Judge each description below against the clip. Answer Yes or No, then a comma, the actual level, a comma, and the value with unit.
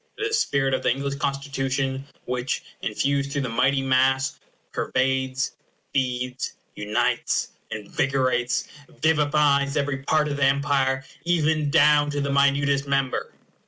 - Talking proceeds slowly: Yes, slow, 130 wpm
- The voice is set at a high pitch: No, medium, 140 Hz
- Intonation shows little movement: Yes, narrow, 1.4 semitones